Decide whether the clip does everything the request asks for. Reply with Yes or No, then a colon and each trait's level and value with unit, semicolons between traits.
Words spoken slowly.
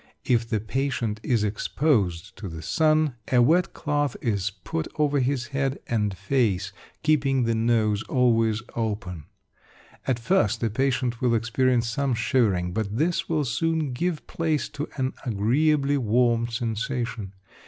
No: average, 145 wpm